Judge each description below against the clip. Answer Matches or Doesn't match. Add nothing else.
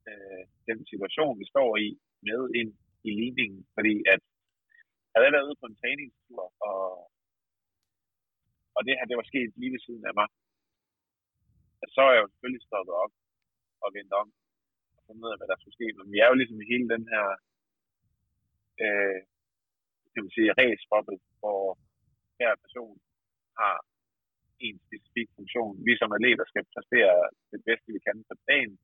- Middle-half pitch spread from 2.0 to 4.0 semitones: Matches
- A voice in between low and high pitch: Doesn't match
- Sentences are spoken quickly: Doesn't match